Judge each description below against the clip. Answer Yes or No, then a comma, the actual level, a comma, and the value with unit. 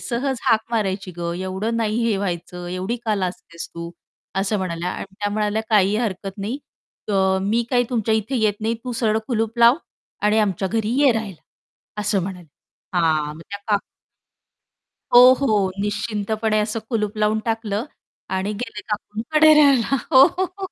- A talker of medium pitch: No, high, 210 Hz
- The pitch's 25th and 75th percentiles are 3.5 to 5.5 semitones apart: No, average, 3.0 semitones